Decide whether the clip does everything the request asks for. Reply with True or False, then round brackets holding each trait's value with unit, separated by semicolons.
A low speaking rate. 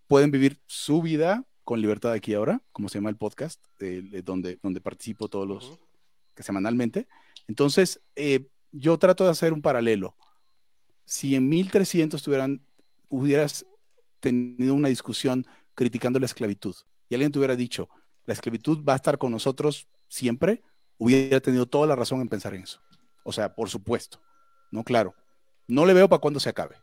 False (170 wpm)